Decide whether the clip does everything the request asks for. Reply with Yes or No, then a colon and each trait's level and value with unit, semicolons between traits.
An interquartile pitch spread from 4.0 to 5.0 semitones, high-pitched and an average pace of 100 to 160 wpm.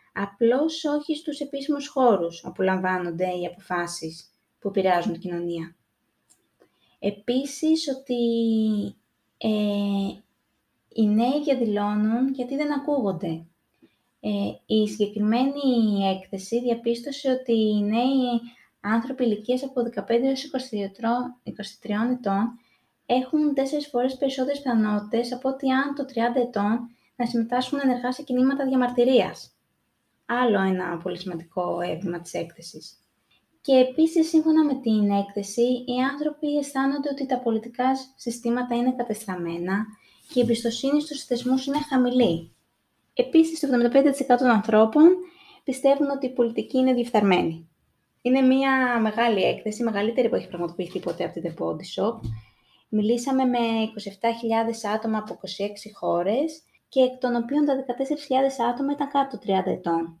Yes: average, 4.5 semitones; high, 240 Hz; average, 125 wpm